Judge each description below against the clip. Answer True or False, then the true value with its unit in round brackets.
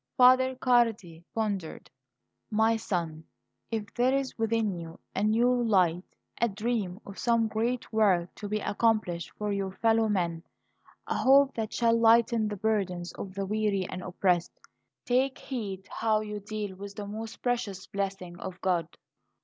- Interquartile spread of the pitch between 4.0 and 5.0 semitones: False (3.3 semitones)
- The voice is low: False (210 Hz)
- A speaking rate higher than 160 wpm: False (155 wpm)